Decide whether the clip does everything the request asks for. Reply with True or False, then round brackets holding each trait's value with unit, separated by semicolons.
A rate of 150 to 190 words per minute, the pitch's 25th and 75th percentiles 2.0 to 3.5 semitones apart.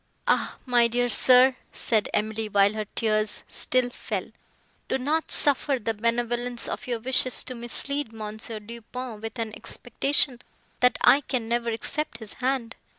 True (155 wpm; 2.4 semitones)